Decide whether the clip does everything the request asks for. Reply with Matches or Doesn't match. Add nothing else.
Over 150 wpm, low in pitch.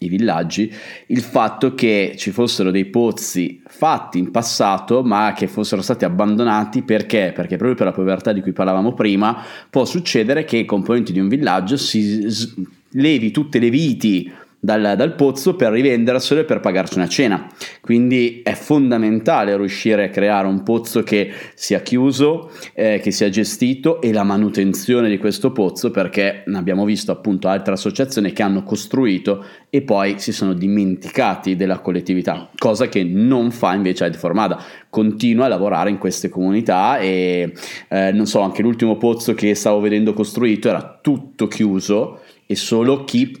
Matches